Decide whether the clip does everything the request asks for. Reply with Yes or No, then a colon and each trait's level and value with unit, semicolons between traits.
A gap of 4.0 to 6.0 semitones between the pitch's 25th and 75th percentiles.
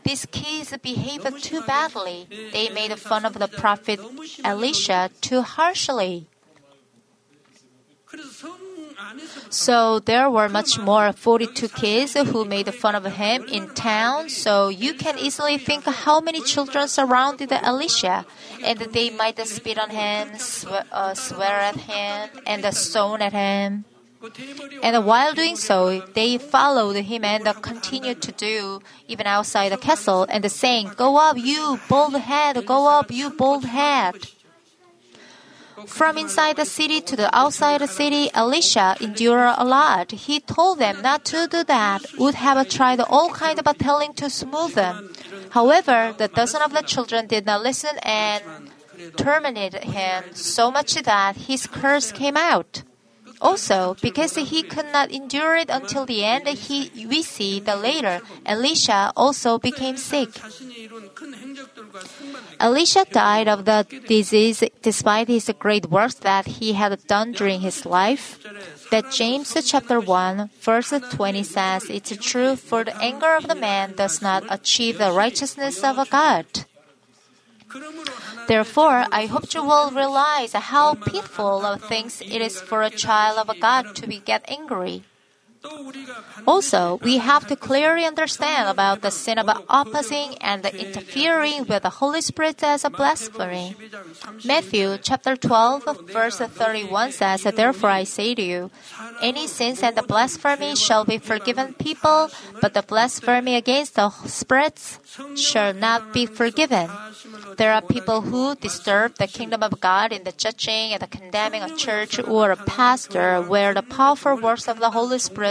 Yes: average, 5.2 semitones